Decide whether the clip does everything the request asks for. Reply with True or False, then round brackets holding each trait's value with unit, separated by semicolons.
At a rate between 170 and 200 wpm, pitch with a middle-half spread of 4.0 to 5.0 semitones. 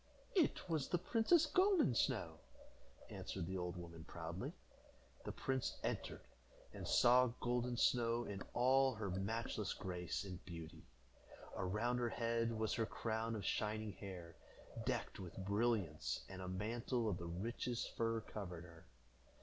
False (140 wpm; 4.7 semitones)